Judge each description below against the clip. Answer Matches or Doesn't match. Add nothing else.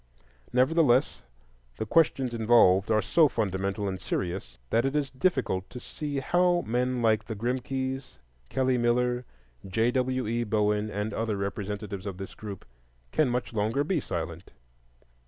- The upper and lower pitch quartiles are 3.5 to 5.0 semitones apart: Matches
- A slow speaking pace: Doesn't match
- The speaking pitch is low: Matches